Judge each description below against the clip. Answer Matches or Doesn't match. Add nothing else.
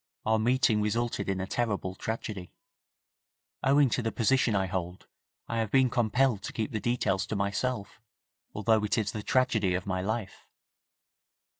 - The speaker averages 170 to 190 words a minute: Doesn't match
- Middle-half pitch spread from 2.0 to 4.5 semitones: Matches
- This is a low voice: Matches